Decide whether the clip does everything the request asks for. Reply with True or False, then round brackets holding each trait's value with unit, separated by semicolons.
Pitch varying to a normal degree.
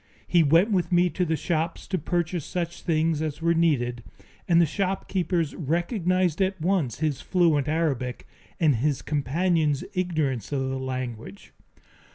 True (3.6 semitones)